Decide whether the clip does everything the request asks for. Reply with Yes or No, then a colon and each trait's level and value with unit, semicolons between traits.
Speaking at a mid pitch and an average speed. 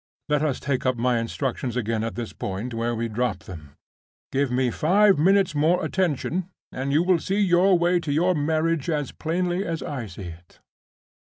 Yes: medium, 145 Hz; average, 185 wpm